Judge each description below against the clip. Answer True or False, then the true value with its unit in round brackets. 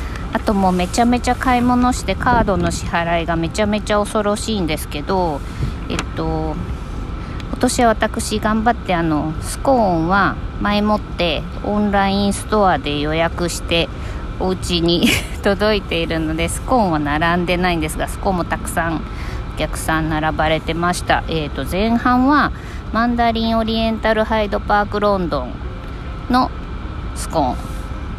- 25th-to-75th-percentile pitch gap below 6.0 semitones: True (5.4 semitones)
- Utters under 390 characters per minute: True (315 characters per minute)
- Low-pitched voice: False (200 Hz)